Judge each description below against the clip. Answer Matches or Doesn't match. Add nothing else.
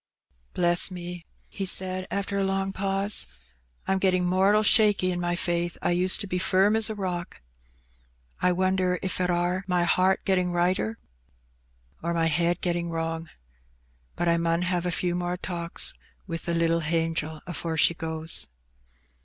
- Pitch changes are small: Matches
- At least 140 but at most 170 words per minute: Matches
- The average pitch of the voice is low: Doesn't match